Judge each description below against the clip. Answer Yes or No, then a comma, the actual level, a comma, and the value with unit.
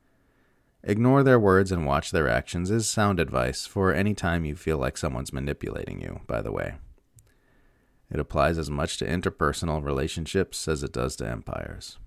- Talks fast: No, average, 170 wpm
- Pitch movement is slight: No, average, 5.0 semitones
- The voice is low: Yes, very low, 85 Hz